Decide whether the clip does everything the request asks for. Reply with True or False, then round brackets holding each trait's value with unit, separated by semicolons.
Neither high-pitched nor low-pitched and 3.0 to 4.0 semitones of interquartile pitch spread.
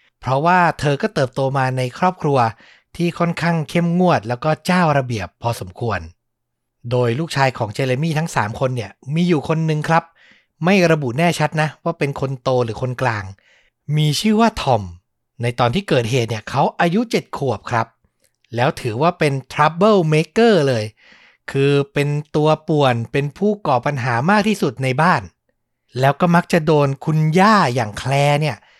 False (145 Hz; 5.3 semitones)